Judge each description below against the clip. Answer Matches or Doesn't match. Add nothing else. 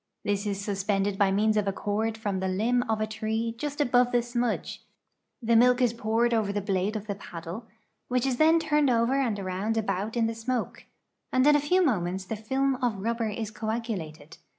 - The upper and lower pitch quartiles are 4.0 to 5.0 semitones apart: Doesn't match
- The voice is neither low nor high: Doesn't match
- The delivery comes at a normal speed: Doesn't match